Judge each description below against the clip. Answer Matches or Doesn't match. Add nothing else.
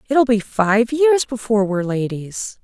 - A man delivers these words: Doesn't match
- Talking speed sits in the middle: Matches